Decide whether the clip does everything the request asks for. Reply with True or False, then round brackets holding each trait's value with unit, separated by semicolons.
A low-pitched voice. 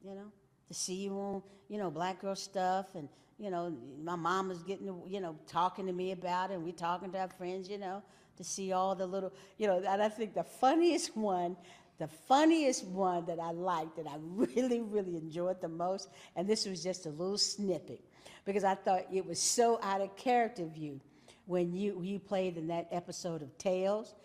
False (185 Hz)